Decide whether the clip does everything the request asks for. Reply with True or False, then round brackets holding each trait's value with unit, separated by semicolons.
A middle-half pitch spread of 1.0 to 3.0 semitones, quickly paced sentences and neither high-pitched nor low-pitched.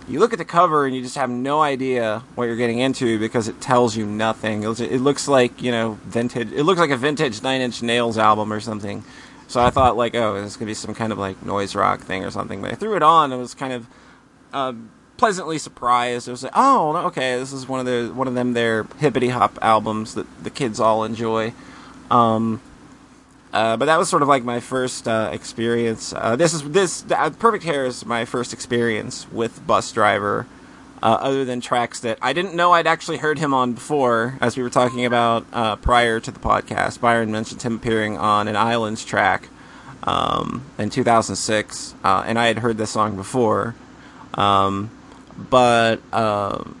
False (2.7 semitones; 215 wpm; 120 Hz)